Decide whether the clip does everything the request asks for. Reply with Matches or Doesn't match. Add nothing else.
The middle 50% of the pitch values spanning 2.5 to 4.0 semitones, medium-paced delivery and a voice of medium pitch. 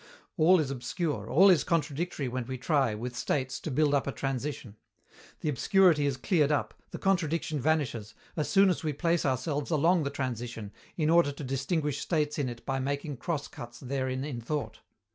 Matches